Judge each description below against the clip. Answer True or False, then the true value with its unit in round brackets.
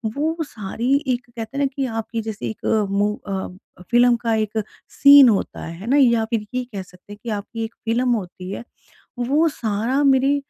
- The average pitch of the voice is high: True (230 Hz)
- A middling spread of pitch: True (3.9 semitones)